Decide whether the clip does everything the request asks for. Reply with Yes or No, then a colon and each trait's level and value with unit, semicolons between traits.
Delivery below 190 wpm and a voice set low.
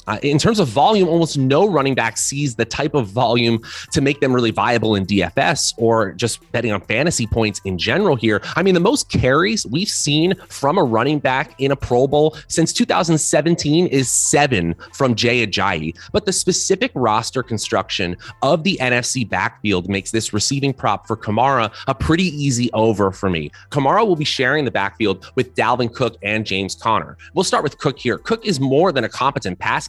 No: average, 195 wpm; low, 125 Hz